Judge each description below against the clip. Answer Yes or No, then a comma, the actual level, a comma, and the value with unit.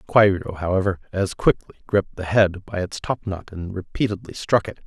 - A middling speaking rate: Yes, average, 175 wpm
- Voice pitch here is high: No, very low, 95 Hz